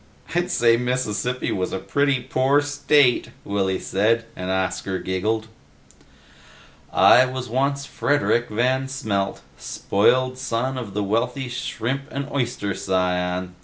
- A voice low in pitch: Yes, low, 120 Hz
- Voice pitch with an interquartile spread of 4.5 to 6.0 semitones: Yes, average, 4.9 semitones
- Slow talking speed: Yes, slow, 125 wpm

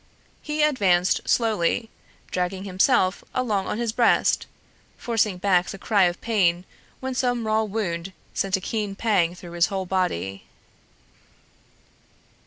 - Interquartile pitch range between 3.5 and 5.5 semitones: Yes, average, 3.8 semitones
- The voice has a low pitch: No, high, 195 Hz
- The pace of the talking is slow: Yes, slow, 130 wpm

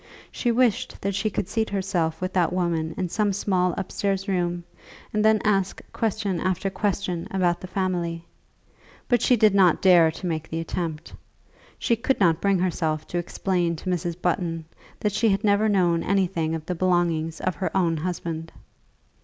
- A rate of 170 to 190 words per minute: Yes, average, 175 wpm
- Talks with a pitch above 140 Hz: Yes, medium, 185 Hz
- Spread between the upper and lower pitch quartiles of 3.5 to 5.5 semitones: No, average, 2.9 semitones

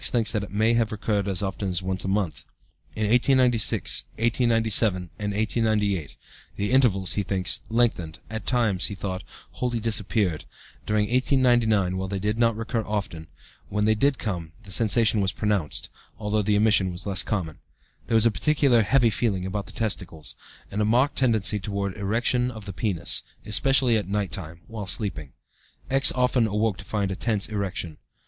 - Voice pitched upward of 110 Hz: No, low, 105 Hz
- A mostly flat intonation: No, average, 3.0 semitones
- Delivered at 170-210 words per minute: Yes, average, 175 wpm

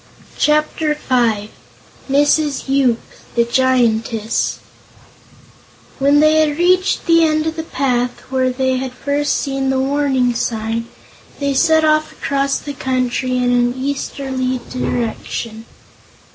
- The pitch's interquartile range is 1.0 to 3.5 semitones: Yes, average, 2.9 semitones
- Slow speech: Yes, slow, 120 wpm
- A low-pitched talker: No, very high, 265 Hz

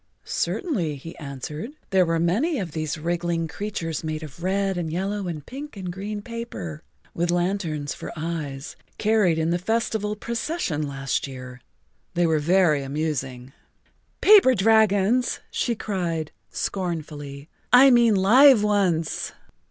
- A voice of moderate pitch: Yes, medium, 175 Hz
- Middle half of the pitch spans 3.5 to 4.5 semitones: No, average, 5.3 semitones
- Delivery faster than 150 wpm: No, slow, 135 wpm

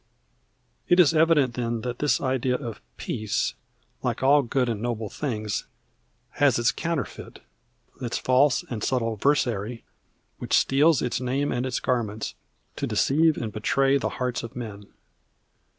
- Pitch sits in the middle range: No, low, 125 Hz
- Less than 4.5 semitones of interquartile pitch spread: Yes, average, 3.4 semitones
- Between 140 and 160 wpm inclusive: Yes, average, 145 wpm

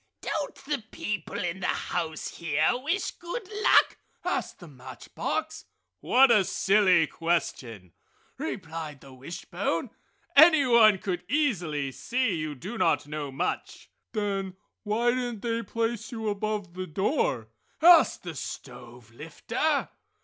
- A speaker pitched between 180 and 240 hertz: Yes, high, 190 Hz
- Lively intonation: Yes, wide, 7.2 semitones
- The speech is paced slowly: Yes, slow, 125 wpm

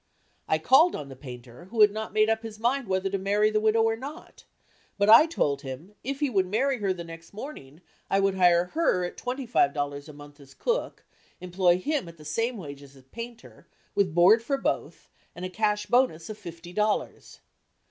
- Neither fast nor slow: No, fast, 210 wpm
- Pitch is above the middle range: Yes, high, 195 Hz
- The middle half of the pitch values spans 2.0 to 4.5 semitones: No, wide, 5.6 semitones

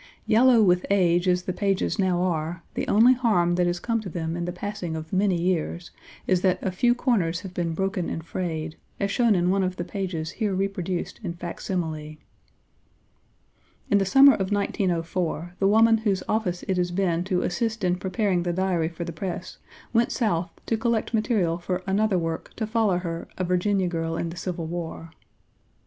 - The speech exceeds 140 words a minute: Yes, average, 190 wpm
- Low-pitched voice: No, medium, 180 Hz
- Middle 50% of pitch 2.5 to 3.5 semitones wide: Yes, average, 2.8 semitones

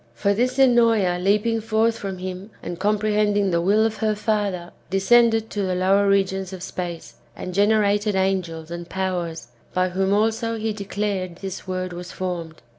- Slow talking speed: No, average, 170 wpm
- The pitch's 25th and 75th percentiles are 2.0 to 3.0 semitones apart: Yes, average, 2.7 semitones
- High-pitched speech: Yes, high, 195 Hz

